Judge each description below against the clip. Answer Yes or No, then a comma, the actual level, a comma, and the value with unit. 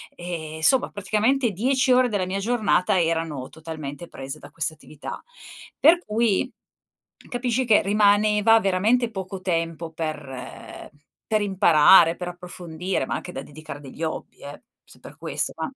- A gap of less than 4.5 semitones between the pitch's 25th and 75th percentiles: No, average, 5.2 semitones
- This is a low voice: No, medium, 185 Hz